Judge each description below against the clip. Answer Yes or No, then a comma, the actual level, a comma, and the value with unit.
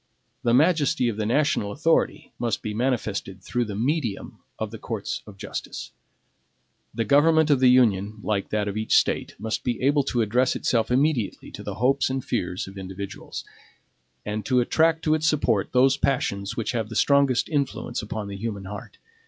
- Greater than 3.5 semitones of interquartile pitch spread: Yes, average, 4.6 semitones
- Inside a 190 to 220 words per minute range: No, average, 180 wpm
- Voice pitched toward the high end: No, low, 120 Hz